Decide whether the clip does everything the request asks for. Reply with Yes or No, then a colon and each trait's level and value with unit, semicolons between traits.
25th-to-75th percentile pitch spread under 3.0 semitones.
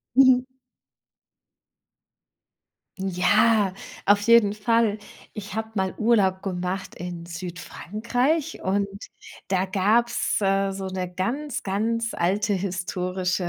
No: average, 3.4 semitones